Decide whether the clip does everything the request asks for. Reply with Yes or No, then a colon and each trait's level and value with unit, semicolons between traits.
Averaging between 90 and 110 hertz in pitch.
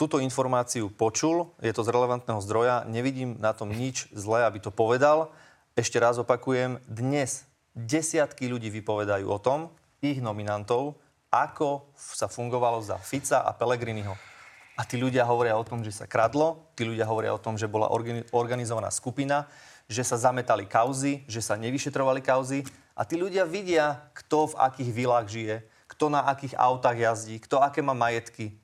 No: low, 125 Hz